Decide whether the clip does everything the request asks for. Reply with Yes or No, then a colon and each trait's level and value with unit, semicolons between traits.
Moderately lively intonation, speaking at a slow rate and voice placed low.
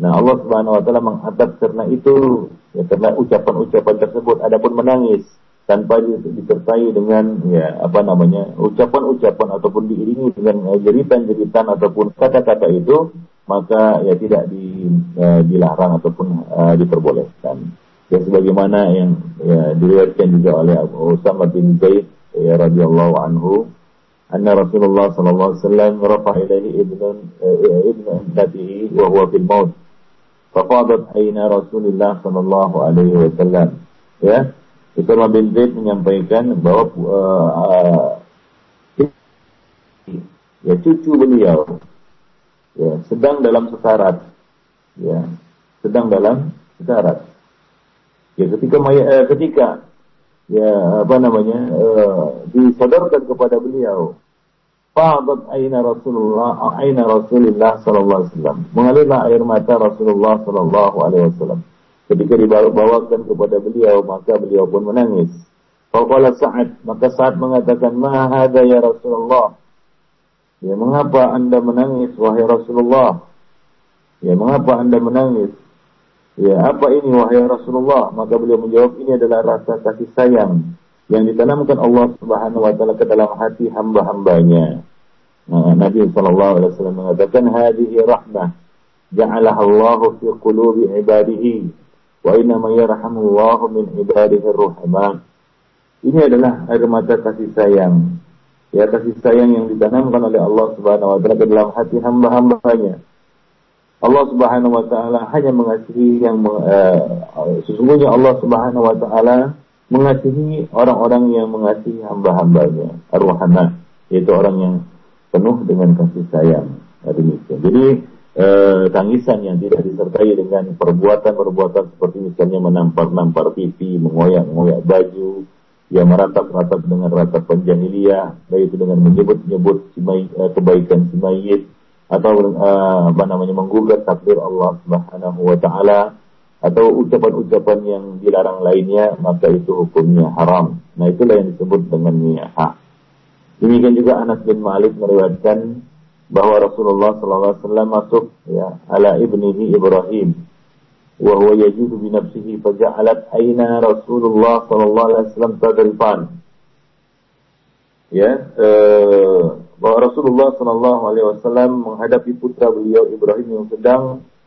Yes: average, 5.0 semitones; slow, 110 wpm; low, 110 Hz